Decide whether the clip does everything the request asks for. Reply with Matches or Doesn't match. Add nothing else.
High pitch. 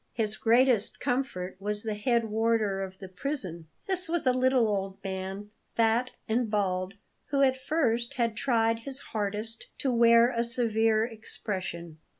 Matches